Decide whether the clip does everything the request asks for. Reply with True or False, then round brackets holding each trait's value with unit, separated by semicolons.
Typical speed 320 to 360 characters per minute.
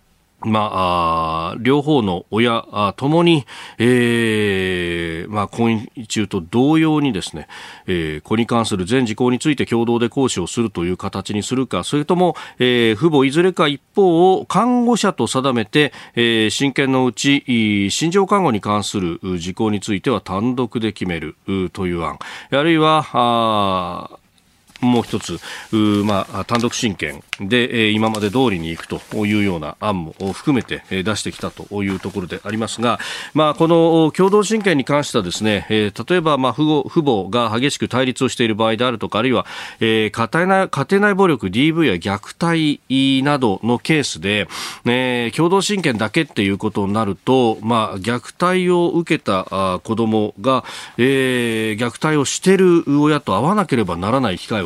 False (300 characters per minute)